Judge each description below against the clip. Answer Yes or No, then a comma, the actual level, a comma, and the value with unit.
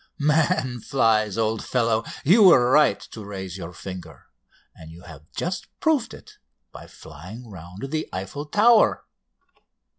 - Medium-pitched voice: No, low, 115 Hz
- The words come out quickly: No, average, 140 wpm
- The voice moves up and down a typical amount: No, wide, 8.2 semitones